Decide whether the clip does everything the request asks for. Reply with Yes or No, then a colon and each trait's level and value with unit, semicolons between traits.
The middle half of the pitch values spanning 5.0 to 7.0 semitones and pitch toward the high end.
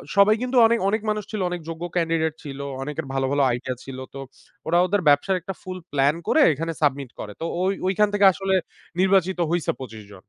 No: wide, 5.5 semitones; medium, 165 Hz